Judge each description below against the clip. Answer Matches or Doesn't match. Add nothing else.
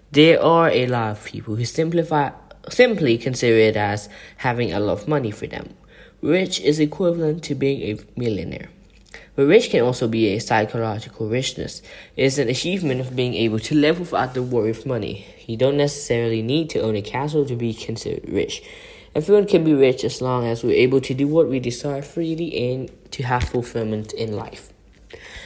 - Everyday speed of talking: Matches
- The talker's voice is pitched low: Matches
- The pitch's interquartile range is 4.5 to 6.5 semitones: Matches